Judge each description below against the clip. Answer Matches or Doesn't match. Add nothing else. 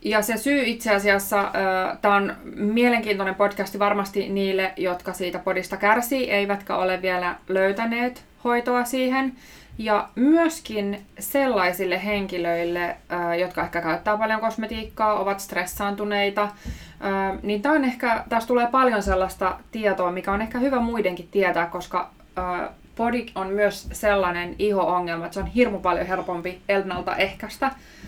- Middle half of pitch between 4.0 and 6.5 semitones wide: Doesn't match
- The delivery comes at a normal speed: Matches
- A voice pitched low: Doesn't match